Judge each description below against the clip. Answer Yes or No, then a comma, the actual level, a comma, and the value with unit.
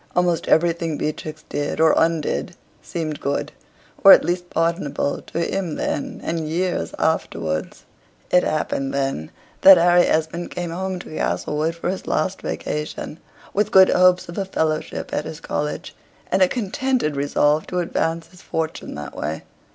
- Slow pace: No, average, 155 wpm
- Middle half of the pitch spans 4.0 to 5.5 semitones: No, average, 2.8 semitones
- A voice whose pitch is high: No, medium, 165 Hz